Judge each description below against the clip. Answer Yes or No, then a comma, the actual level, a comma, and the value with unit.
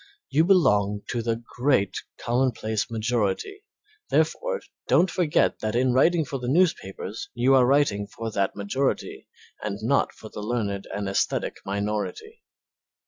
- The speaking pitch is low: Yes, low, 120 Hz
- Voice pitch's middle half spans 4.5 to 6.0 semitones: Yes, average, 5.3 semitones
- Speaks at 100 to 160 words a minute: Yes, average, 140 wpm